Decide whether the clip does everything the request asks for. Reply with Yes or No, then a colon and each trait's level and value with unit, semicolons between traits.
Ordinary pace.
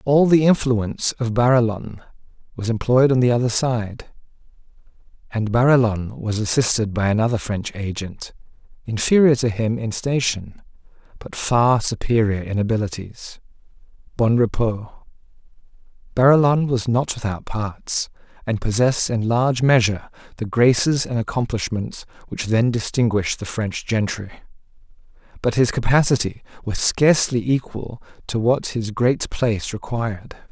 No: slow, 120 wpm